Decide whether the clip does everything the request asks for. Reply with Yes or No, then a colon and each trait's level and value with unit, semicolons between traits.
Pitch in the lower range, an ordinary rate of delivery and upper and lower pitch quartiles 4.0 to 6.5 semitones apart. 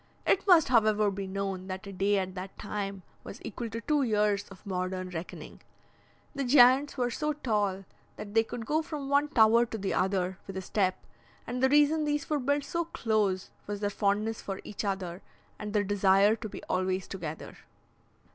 No: high, 210 Hz; average, 190 wpm; average, 4.7 semitones